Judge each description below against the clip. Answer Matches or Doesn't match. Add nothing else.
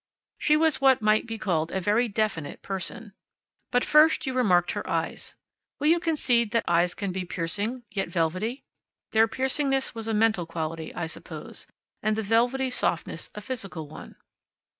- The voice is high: Matches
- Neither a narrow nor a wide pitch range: Doesn't match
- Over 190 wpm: Doesn't match